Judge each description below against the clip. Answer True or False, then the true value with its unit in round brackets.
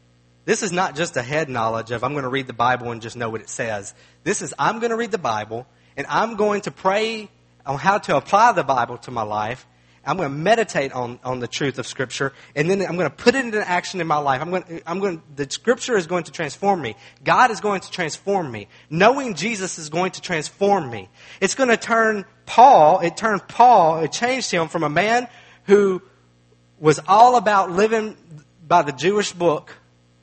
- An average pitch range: False (7.8 semitones)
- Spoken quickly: True (225 wpm)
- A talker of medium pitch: True (170 Hz)